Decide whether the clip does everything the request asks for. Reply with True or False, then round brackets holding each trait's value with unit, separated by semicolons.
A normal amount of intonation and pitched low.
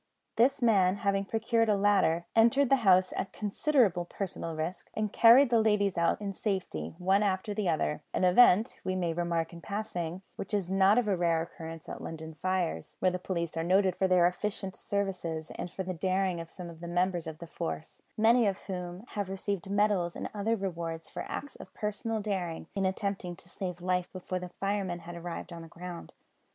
False (3.0 semitones; 185 Hz)